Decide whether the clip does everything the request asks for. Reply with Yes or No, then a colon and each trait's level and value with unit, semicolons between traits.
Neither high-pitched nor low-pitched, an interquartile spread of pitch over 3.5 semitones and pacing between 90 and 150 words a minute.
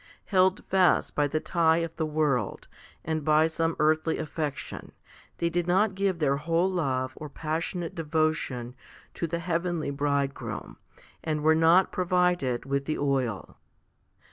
No: medium, 160 Hz; average, 2.9 semitones; average, 145 wpm